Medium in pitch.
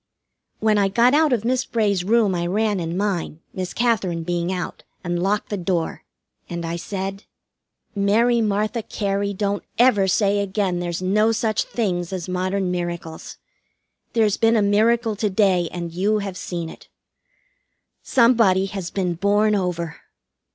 No: high, 200 Hz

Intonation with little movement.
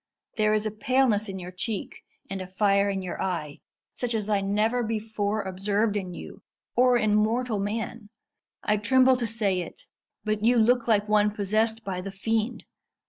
Yes: narrow, 2.3 semitones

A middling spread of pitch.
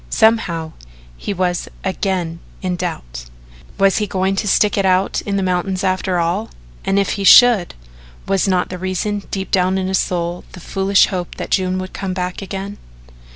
No: narrow, 1.5 semitones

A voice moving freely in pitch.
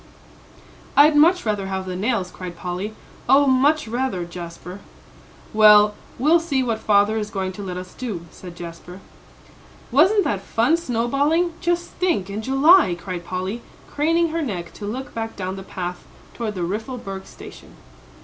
Yes: wide, 6.8 semitones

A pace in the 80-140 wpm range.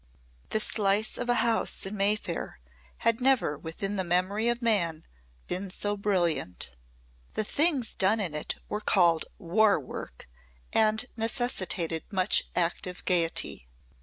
Yes: slow, 135 wpm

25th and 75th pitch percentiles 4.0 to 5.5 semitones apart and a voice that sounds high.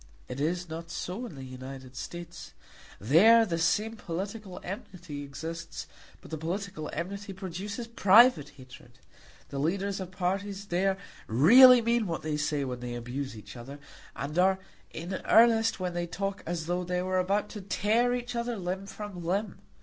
No: average, 4.7 semitones; medium, 180 Hz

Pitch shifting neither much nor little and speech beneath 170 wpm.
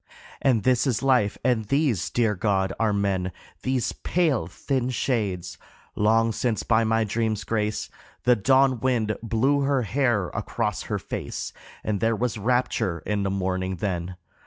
Yes: average, 3.9 semitones; average, 155 wpm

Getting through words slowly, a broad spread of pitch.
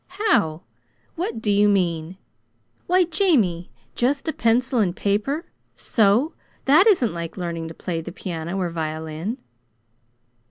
Yes: slow, 130 wpm; wide, 8.4 semitones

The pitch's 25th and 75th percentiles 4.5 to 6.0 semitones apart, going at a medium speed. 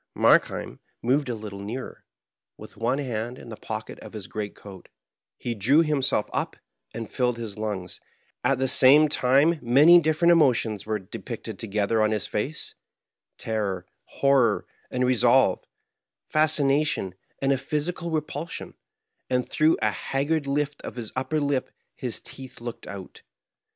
Yes: average, 5.1 semitones; average, 150 wpm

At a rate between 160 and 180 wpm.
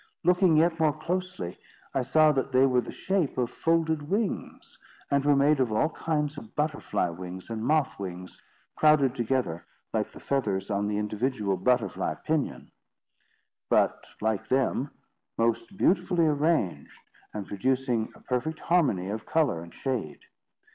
No: average, 150 wpm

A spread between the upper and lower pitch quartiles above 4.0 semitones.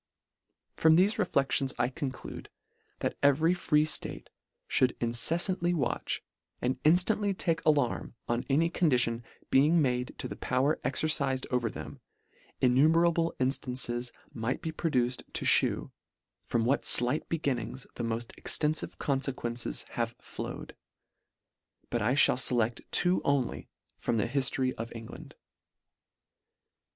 Yes: average, 4.5 semitones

